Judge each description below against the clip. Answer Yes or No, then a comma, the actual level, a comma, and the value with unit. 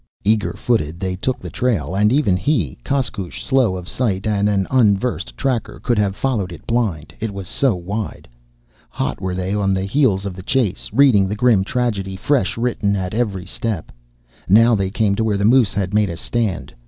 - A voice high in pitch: No, low, 105 Hz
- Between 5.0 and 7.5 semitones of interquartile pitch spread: No, average, 3.9 semitones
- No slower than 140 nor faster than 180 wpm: No, average, 195 wpm